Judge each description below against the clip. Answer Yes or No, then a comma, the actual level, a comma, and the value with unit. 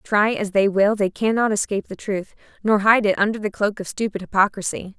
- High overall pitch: Yes, high, 205 Hz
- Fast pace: Yes, fast, 215 wpm